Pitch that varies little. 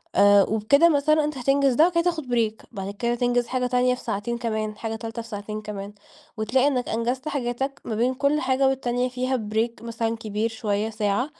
No: average, 3.2 semitones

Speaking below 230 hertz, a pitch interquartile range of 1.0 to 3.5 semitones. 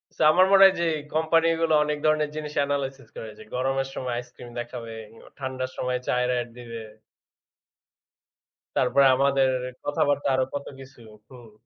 Yes: low, 135 Hz; average, 3.1 semitones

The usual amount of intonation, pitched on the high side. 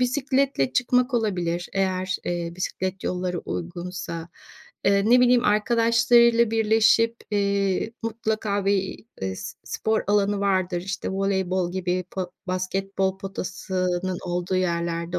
Yes: average, 3.3 semitones; high, 195 Hz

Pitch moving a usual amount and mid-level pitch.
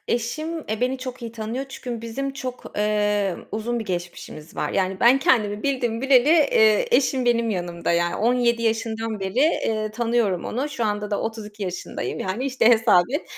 No: average, 3.4 semitones; high, 225 Hz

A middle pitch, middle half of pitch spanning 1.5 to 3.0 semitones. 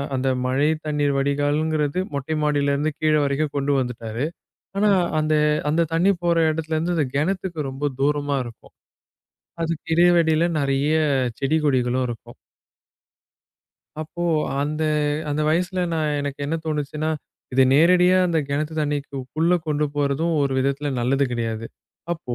Yes: medium, 150 Hz; narrow, 2.4 semitones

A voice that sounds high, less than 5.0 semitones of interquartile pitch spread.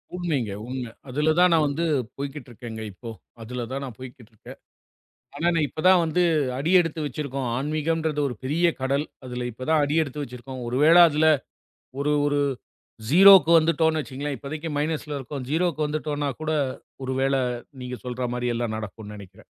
No: medium, 145 Hz; average, 3.9 semitones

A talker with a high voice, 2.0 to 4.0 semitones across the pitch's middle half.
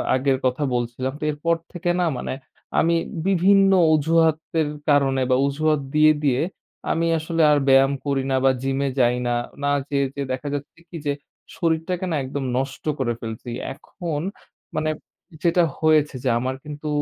No: medium, 145 Hz; average, 3.4 semitones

